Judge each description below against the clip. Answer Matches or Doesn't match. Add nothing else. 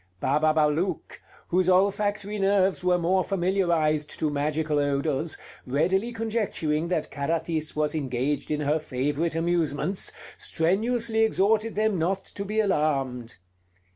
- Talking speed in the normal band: Doesn't match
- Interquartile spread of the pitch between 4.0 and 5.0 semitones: Matches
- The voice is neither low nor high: Matches